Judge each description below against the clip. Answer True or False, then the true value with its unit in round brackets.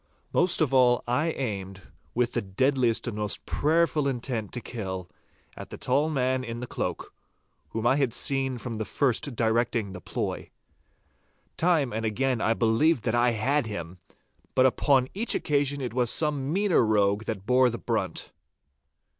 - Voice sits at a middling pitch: False (125 Hz)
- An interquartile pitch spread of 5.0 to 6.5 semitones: False (3.7 semitones)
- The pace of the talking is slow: False (165 wpm)